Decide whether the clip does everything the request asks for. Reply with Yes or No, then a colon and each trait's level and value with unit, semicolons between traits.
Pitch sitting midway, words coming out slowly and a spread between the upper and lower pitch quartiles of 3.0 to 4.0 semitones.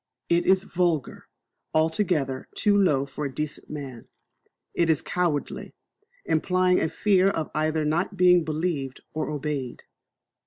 Yes: medium, 160 Hz; slow, 130 wpm; average, 3.6 semitones